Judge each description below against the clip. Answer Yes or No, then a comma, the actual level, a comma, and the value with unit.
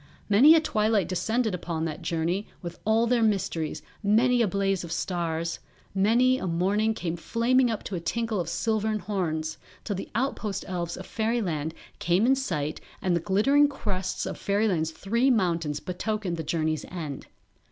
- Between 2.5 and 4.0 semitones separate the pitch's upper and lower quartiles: No, average, 4.8 semitones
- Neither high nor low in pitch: No, high, 195 Hz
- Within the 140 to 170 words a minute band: Yes, average, 165 wpm